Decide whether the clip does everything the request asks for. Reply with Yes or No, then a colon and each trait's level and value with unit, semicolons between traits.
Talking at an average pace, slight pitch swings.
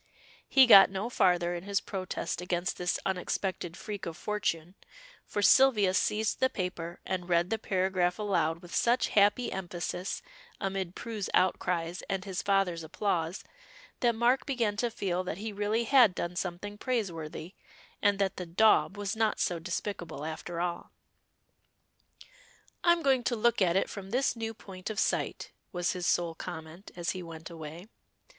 No: average, 160 wpm; average, 3.3 semitones